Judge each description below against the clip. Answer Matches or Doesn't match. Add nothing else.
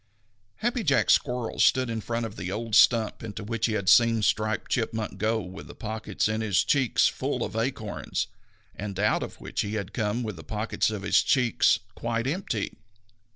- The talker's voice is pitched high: Doesn't match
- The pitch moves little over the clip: Matches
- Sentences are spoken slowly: Doesn't match